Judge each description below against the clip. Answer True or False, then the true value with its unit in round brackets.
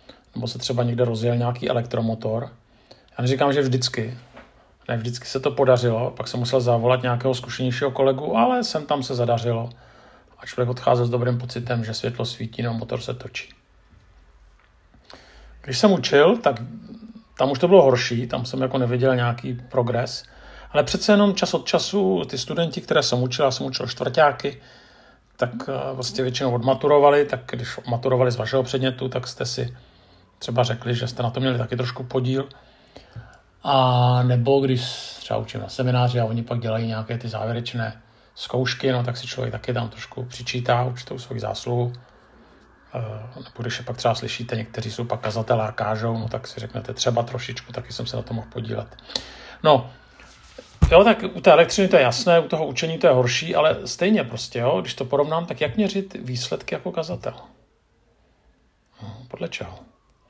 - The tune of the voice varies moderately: False (1.9 semitones)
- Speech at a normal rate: False (175 wpm)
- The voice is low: True (125 Hz)